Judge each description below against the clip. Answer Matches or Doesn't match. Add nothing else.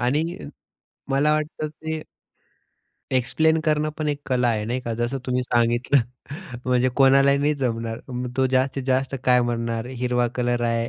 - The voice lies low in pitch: Matches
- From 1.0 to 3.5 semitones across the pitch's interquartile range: Matches